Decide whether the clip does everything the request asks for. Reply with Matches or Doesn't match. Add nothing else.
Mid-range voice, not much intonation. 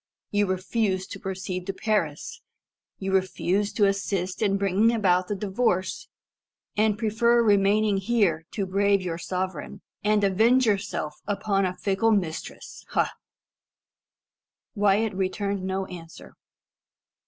Doesn't match